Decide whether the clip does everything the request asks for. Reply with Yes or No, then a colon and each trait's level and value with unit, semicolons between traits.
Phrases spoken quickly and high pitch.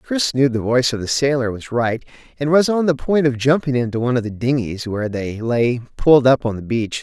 No: fast, 250 wpm; low, 125 Hz